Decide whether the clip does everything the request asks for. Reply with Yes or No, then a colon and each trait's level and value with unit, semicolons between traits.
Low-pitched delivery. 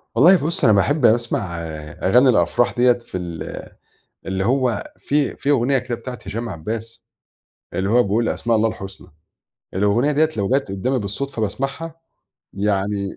Yes: low, 115 Hz